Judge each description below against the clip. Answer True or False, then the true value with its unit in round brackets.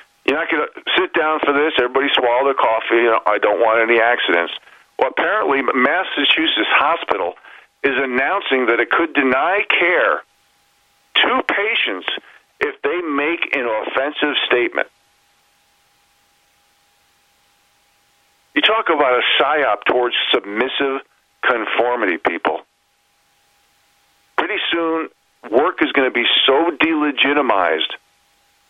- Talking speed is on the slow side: True (115 wpm)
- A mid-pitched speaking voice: True (160 Hz)